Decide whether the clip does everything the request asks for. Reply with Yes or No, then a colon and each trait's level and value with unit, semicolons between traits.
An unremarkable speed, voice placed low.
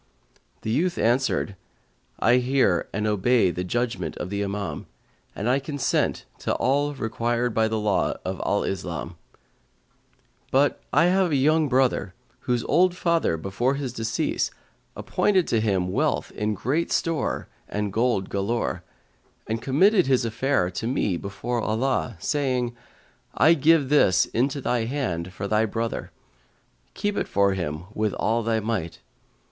Yes: average, 150 wpm; low, 115 Hz